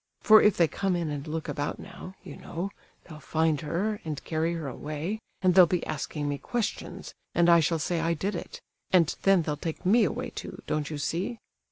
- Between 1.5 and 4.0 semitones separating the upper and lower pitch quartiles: Yes, average, 3.6 semitones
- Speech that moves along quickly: Yes, fast, 210 wpm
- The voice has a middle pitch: Yes, medium, 165 Hz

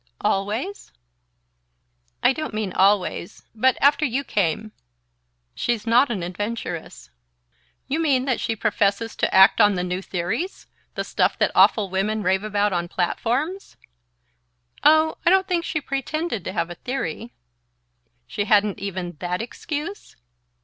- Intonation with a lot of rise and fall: Yes, wide, 6.3 semitones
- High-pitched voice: Yes, high, 215 Hz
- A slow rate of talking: No, average, 145 wpm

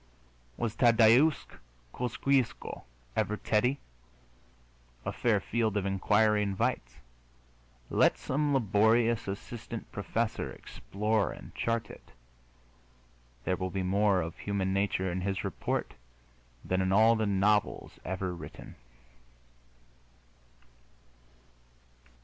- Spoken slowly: Yes, slow, 100 wpm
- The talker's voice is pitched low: Yes, low, 105 Hz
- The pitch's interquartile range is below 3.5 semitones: Yes, average, 3.1 semitones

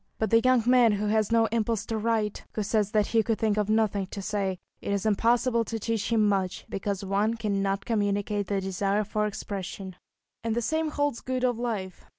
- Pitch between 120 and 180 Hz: No, high, 215 Hz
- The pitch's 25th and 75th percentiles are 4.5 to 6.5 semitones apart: No, narrow, 2.4 semitones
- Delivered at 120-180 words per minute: No, fast, 205 wpm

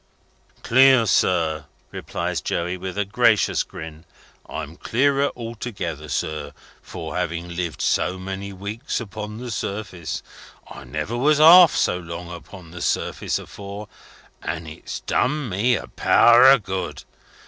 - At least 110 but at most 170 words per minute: Yes, slow, 135 wpm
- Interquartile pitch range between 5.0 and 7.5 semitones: Yes, wide, 5.6 semitones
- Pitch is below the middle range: Yes, low, 100 Hz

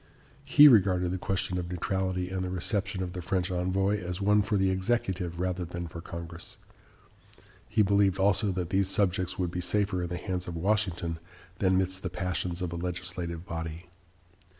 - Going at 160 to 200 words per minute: Yes, average, 180 wpm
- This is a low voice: Yes, very low, 90 Hz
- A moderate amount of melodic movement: No, narrow, 1.7 semitones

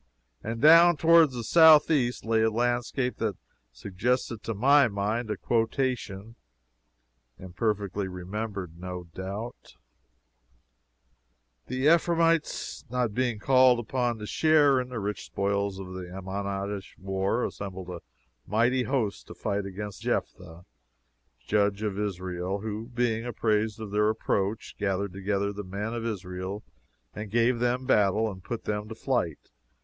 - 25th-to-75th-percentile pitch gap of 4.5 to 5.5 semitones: No, average, 3.8 semitones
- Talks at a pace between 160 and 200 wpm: No, slow, 135 wpm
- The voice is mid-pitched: No, low, 105 Hz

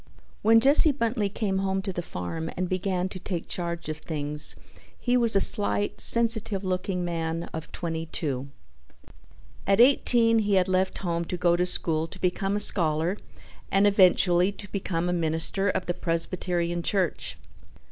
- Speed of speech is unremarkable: Yes, average, 165 wpm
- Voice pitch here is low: No, medium, 185 Hz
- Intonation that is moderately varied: Yes, average, 3.2 semitones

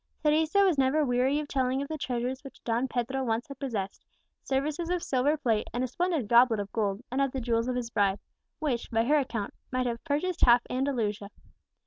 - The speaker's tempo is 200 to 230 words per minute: Yes, fast, 205 wpm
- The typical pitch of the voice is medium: No, very high, 255 Hz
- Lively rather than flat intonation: No, average, 3.5 semitones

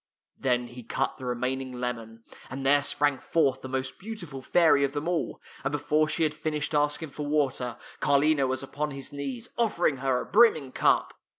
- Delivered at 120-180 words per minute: No, average, 190 wpm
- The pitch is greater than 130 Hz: Yes, medium, 140 Hz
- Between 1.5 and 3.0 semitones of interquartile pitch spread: Yes, narrow, 2.6 semitones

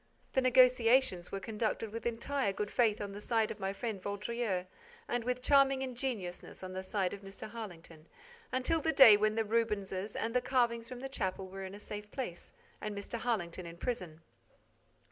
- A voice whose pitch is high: Yes, high, 215 Hz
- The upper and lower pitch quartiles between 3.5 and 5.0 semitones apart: Yes, average, 4.1 semitones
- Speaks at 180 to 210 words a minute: Yes, average, 185 wpm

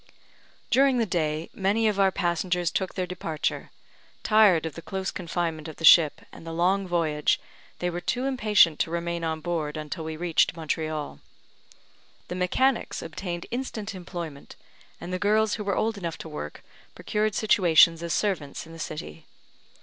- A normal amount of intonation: Yes, average, 3.6 semitones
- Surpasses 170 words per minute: No, average, 165 wpm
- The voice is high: No, medium, 175 Hz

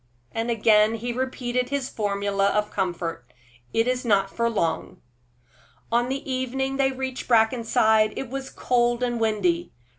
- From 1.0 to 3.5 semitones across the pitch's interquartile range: Yes, average, 3.2 semitones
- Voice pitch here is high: Yes, high, 235 Hz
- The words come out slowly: No, average, 145 wpm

